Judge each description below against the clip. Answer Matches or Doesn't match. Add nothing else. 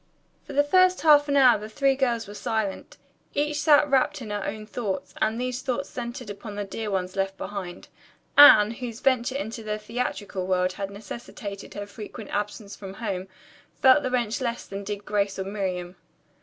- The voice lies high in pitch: Matches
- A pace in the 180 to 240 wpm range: Matches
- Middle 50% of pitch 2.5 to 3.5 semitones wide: Doesn't match